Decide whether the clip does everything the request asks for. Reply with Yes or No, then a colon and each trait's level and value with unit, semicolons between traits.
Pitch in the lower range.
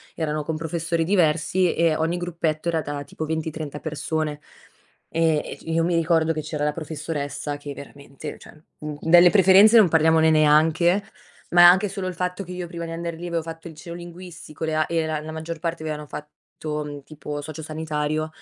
No: medium, 160 Hz